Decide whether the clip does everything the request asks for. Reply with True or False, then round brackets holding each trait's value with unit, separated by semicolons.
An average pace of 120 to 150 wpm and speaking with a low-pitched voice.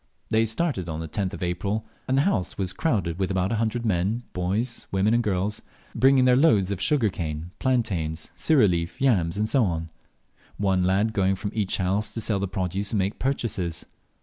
False (190 wpm; 100 Hz)